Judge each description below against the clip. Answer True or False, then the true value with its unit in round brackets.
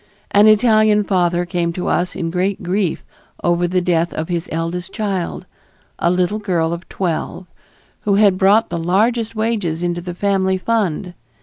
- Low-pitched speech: False (180 Hz)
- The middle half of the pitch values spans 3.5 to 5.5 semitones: False (2.9 semitones)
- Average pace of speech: True (165 wpm)